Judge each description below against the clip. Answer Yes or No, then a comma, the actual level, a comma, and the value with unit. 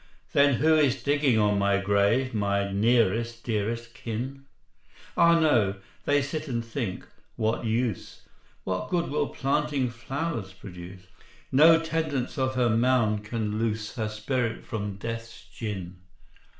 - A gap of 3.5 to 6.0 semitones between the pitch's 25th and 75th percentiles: Yes, average, 4.5 semitones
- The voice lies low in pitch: Yes, low, 115 Hz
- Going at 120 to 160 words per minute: Yes, slow, 135 wpm